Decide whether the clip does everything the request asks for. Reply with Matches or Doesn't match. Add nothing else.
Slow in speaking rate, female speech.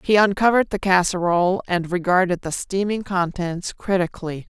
Matches